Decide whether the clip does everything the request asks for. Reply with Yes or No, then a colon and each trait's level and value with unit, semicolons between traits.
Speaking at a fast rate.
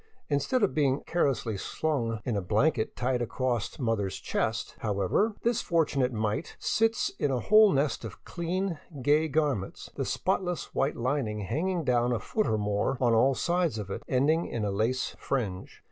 No: average, 175 wpm